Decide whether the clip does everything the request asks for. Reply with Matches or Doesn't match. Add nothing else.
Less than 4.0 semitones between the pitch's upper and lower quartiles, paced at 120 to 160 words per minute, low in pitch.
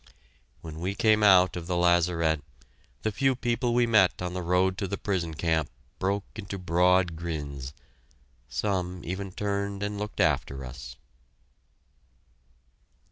Matches